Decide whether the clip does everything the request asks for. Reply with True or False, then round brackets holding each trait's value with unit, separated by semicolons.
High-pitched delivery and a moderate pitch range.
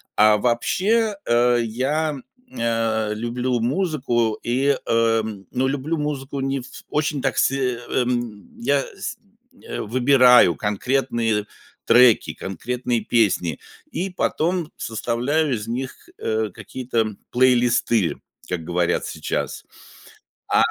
False (125 Hz; 3.3 semitones)